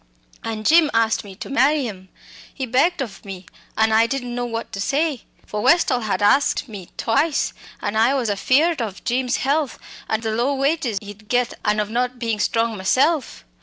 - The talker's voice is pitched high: Yes, high, 240 Hz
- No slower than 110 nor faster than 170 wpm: No, average, 190 wpm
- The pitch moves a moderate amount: Yes, average, 4.1 semitones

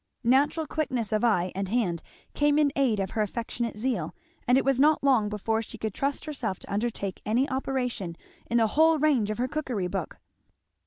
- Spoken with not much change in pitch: No, average, 4.5 semitones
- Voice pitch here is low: No, high, 235 Hz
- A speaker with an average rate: Yes, average, 195 wpm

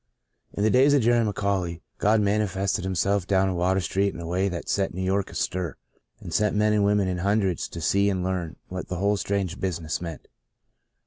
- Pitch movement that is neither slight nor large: No, narrow, 2.1 semitones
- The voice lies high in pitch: No, very low, 95 Hz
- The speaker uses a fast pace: Yes, fast, 210 wpm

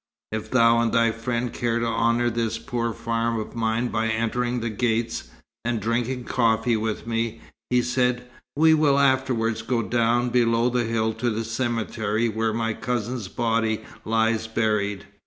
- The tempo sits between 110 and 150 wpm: No, average, 160 wpm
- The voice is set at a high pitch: No, low, 115 Hz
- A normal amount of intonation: No, narrow, 1.4 semitones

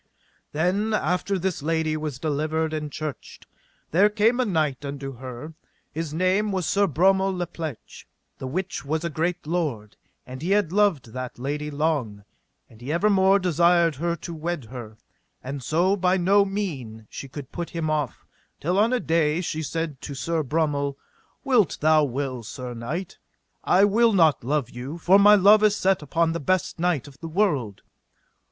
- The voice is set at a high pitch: No, medium, 160 Hz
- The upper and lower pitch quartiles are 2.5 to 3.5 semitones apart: No, average, 4.7 semitones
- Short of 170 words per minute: No, average, 175 wpm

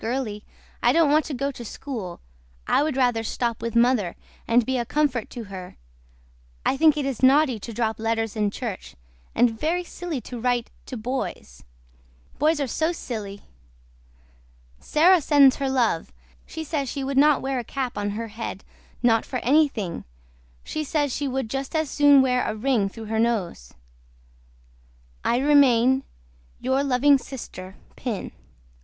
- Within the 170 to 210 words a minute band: No, average, 160 wpm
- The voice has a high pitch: Yes, very high, 255 Hz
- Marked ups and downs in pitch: No, average, 4.0 semitones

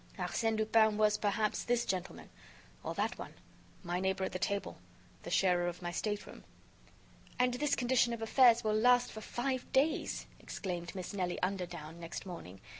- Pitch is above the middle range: Yes, high, 210 Hz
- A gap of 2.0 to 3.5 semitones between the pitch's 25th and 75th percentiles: No, average, 4.8 semitones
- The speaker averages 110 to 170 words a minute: Yes, average, 165 wpm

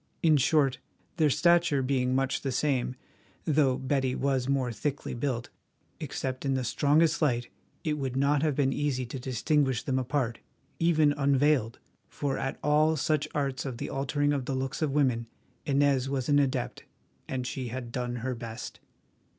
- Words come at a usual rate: Yes, average, 165 wpm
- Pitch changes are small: Yes, narrow, 2.3 semitones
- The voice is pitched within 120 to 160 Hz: Yes, low, 135 Hz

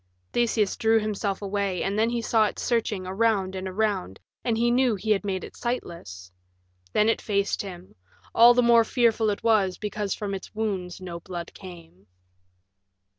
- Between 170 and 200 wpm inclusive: Yes, average, 175 wpm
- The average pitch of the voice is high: Yes, high, 205 Hz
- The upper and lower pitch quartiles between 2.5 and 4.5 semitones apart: Yes, average, 3.3 semitones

